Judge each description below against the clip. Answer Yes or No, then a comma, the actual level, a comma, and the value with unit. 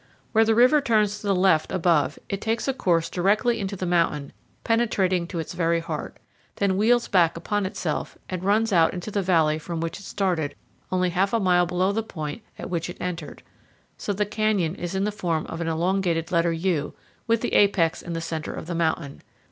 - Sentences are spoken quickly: Yes, fast, 210 wpm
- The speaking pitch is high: No, medium, 180 Hz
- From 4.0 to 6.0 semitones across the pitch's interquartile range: No, average, 3.5 semitones